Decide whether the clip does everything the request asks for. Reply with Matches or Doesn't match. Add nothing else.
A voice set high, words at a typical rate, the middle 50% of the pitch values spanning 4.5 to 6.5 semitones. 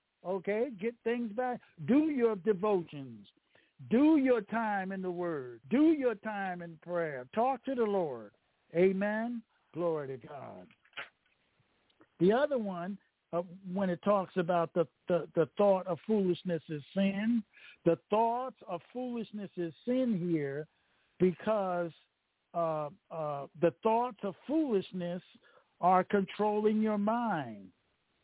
Doesn't match